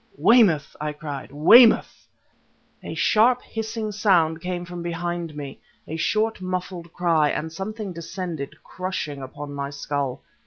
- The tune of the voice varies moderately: Yes, average, 4.4 semitones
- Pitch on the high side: No, medium, 170 Hz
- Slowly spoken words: Yes, slow, 130 wpm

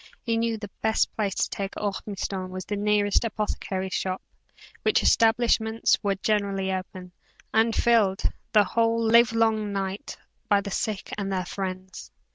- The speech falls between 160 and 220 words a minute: No, average, 150 wpm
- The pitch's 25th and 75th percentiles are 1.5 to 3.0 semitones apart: Yes, narrow, 2.6 semitones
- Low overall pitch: No, high, 205 Hz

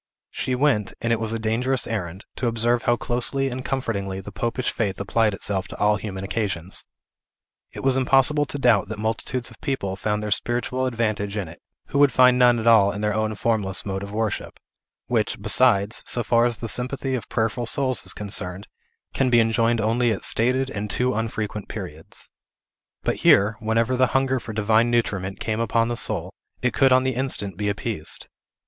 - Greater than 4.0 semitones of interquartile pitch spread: No, average, 3.3 semitones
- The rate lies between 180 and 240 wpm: Yes, average, 195 wpm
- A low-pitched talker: Yes, low, 115 Hz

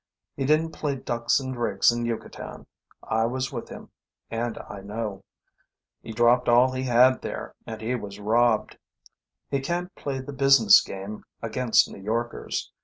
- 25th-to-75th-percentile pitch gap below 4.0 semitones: Yes, average, 2.8 semitones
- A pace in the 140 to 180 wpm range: Yes, average, 160 wpm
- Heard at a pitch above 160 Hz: No, low, 120 Hz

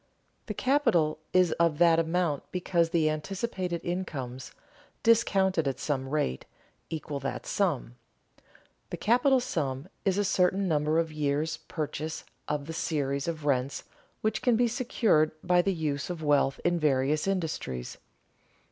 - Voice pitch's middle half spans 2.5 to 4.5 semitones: Yes, average, 4.0 semitones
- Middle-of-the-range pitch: Yes, medium, 160 Hz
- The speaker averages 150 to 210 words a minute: No, average, 140 wpm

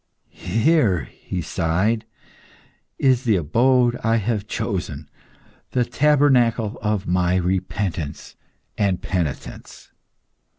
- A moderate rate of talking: No, slow, 90 wpm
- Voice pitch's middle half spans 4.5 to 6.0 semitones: Yes, average, 5.1 semitones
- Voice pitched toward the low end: Yes, low, 105 Hz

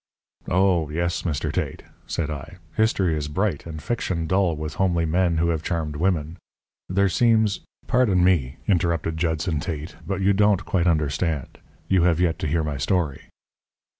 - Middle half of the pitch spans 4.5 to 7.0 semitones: No, average, 3.2 semitones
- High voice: No, very low, 85 Hz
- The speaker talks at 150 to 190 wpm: Yes, average, 165 wpm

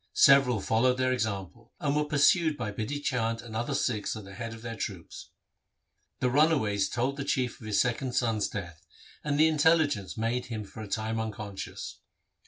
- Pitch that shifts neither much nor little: Yes, average, 4.3 semitones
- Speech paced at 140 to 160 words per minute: No, average, 185 wpm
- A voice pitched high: No, low, 115 Hz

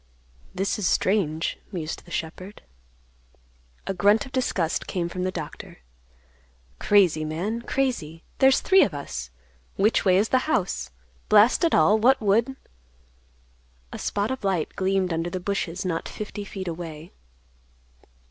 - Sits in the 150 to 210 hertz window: Yes, high, 190 Hz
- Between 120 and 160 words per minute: Yes, average, 140 wpm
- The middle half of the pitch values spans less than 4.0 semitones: No, average, 4.3 semitones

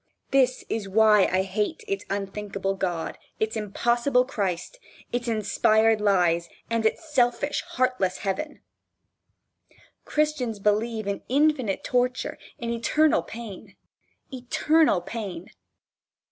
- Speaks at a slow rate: Yes, slow, 105 wpm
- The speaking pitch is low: No, high, 225 Hz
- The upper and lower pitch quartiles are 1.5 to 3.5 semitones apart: No, average, 4.3 semitones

